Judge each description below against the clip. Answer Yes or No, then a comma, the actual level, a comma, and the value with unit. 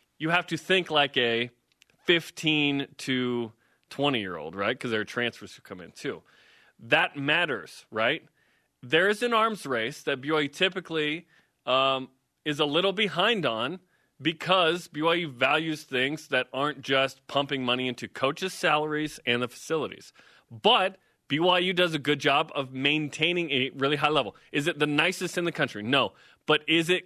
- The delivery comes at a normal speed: Yes, average, 165 wpm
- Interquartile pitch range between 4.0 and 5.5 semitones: Yes, average, 4.6 semitones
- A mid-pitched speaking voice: Yes, medium, 150 Hz